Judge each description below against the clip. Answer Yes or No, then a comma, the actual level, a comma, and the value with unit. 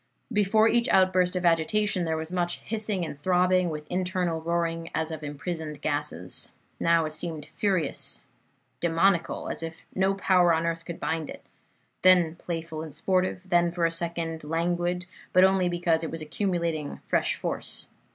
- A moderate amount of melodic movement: No, narrow, 2.2 semitones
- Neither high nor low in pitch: Yes, medium, 170 Hz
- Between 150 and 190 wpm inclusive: Yes, average, 160 wpm